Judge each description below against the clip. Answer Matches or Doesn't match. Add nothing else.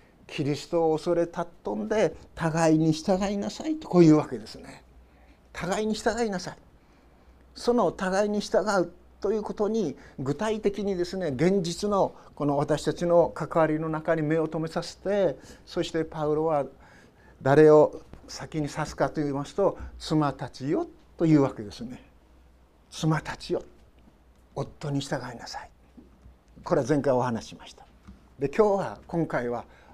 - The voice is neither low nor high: Matches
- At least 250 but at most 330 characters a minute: Matches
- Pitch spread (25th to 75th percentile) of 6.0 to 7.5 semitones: Doesn't match